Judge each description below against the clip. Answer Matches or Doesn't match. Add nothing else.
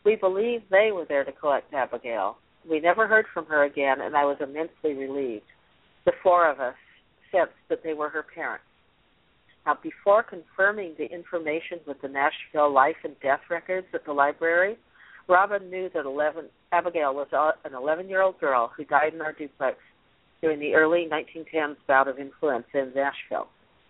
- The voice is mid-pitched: Matches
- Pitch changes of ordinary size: Matches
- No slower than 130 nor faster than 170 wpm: Matches